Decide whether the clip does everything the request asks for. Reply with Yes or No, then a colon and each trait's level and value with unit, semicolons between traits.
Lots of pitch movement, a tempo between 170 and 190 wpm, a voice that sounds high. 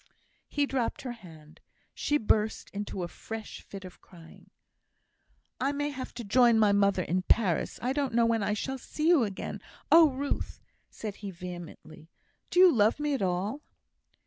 Yes: wide, 5.9 semitones; average, 175 wpm; high, 220 Hz